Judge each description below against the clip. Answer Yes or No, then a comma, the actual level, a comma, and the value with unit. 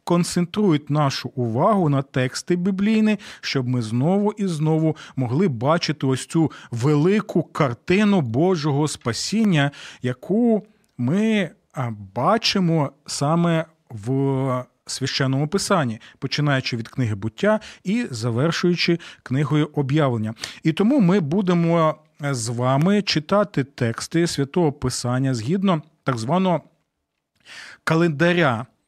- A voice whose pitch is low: No, medium, 155 Hz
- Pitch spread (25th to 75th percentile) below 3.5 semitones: No, wide, 5.6 semitones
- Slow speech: Yes, slow, 100 wpm